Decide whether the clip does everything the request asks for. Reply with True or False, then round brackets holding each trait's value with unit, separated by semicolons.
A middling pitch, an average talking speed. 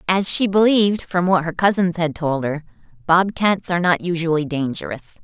True (175 Hz; 170 wpm)